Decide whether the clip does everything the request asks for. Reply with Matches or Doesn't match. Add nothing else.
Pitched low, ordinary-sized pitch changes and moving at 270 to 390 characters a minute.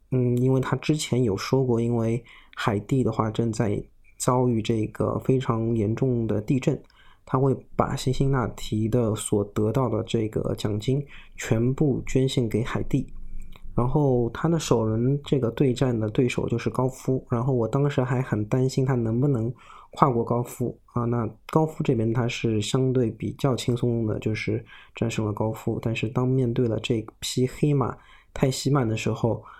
Doesn't match